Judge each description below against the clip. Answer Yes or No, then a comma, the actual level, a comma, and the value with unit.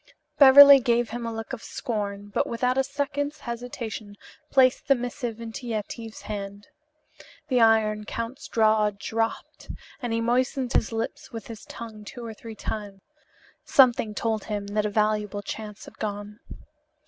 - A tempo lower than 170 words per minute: Yes, average, 155 wpm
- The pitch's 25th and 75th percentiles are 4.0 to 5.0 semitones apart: No, narrow, 2.6 semitones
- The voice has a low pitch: No, high, 225 Hz